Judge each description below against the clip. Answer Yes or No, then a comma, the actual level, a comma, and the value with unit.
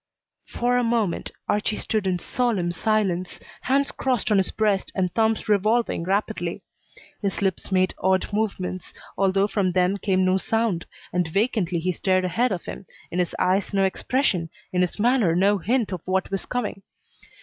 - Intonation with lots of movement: No, average, 3.1 semitones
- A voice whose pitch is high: Yes, high, 195 Hz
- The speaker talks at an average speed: Yes, average, 170 wpm